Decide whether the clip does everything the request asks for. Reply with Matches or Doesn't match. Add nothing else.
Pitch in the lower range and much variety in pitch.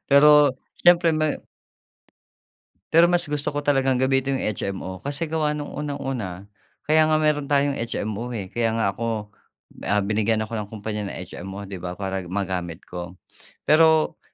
Matches